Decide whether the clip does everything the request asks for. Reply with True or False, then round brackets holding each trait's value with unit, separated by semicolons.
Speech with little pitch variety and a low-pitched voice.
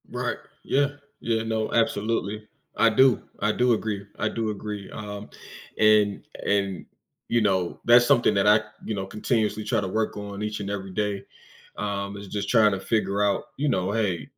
True (1.9 semitones; 105 Hz)